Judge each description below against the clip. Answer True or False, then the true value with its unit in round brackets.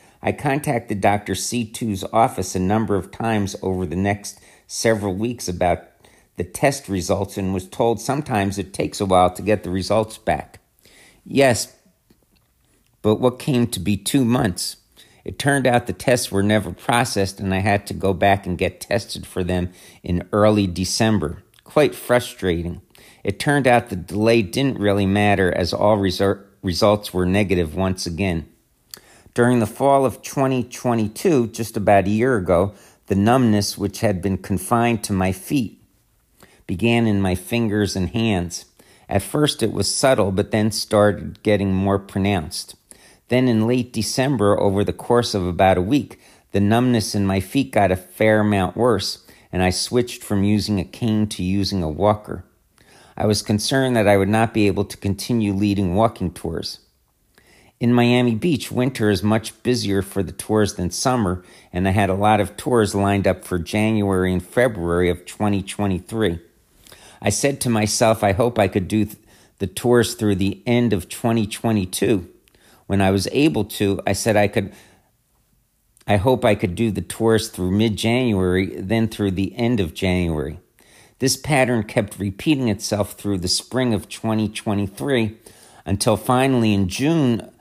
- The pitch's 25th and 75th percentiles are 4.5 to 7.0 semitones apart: False (3.2 semitones)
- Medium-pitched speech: False (105 Hz)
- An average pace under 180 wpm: True (165 wpm)